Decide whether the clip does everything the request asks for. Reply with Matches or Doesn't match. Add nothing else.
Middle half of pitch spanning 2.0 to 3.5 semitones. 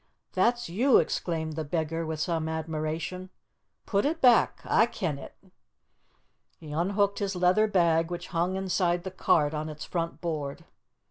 Matches